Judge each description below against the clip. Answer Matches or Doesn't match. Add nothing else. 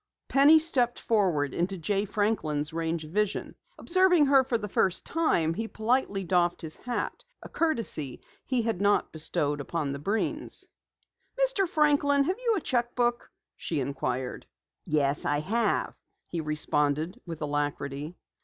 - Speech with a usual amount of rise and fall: Doesn't match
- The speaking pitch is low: Doesn't match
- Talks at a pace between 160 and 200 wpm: Doesn't match